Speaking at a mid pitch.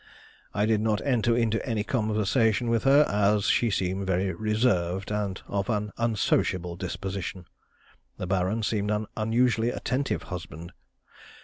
No: low, 105 Hz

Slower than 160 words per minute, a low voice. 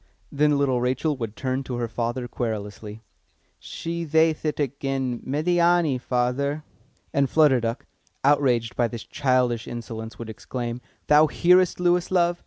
Yes: average, 140 wpm; low, 130 Hz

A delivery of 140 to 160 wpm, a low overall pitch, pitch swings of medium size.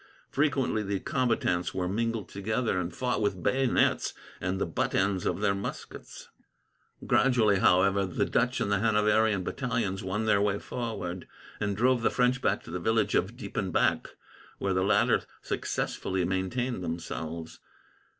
Yes: average, 150 wpm; low, 100 Hz; average, 3.6 semitones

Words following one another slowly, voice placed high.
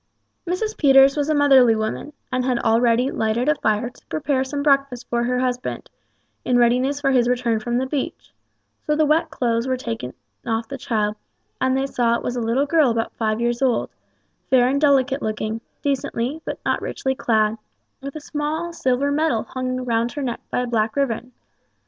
No: average, 195 wpm; very high, 255 Hz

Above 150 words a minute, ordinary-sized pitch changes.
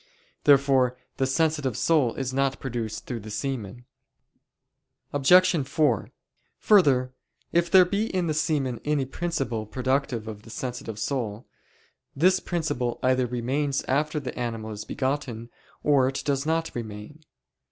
No: slow, 135 wpm; average, 3.9 semitones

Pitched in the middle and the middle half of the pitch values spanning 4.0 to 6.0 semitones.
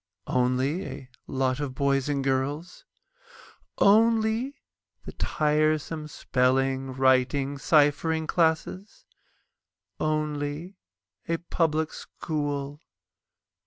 No: medium, 150 Hz; average, 3.4 semitones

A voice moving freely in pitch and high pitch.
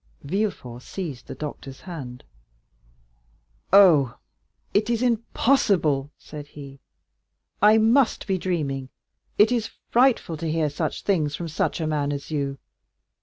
No: wide, 6.6 semitones; medium, 160 Hz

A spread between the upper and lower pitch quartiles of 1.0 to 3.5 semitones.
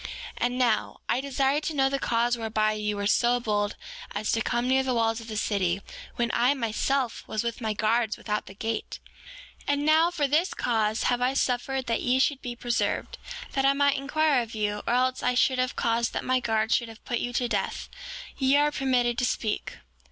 Yes: average, 3.1 semitones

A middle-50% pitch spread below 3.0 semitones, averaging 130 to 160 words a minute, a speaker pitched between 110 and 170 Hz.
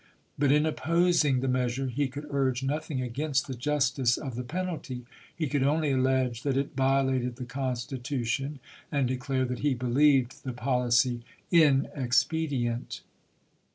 Yes: narrow, 2.4 semitones; average, 140 wpm; low, 135 Hz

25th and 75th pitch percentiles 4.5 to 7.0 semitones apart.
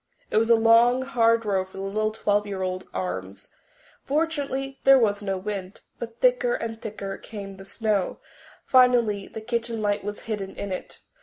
No: average, 3.2 semitones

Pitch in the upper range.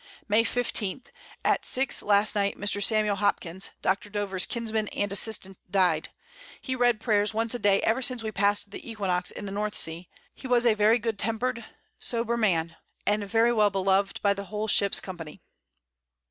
Yes: high, 210 Hz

